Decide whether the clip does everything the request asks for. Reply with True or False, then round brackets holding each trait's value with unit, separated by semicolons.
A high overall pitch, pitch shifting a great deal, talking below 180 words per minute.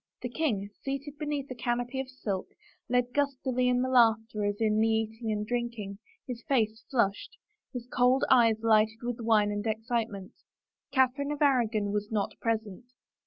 False (235 Hz; 3.0 semitones; 165 wpm)